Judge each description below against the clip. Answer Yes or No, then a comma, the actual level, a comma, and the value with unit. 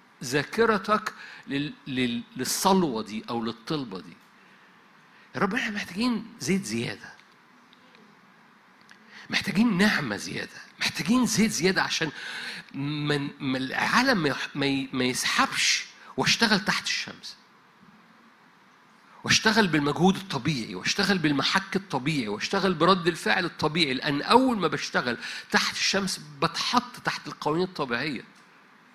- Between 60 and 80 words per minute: No, average, 100 wpm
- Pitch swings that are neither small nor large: No, wide, 6.4 semitones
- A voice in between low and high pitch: Yes, medium, 175 Hz